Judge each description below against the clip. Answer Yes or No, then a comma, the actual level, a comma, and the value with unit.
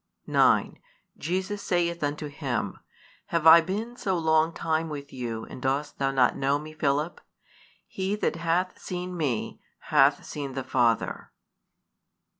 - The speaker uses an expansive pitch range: No, average, 4.0 semitones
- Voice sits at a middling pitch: Yes, medium, 155 Hz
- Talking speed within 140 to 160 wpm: Yes, average, 145 wpm